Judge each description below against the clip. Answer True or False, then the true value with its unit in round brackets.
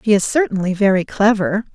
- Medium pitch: False (205 Hz)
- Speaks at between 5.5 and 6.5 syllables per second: True (5.7 syllables/s)